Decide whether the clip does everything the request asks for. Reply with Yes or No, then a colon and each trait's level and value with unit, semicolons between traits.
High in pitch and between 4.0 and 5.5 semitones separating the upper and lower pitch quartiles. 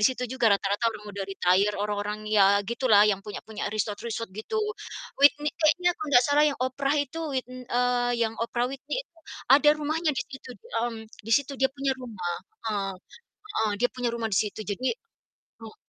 Yes: high, 240 Hz; average, 4.6 semitones